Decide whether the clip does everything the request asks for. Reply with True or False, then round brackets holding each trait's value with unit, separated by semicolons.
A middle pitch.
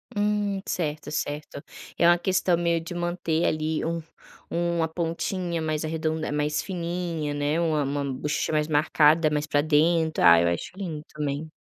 True (160 Hz)